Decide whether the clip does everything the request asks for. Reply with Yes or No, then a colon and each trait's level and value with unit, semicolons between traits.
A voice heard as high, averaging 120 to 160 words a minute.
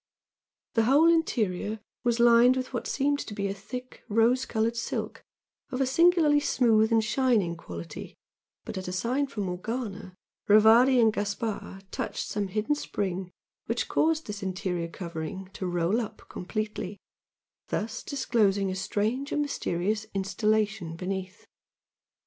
Yes: high, 215 Hz; average, 140 wpm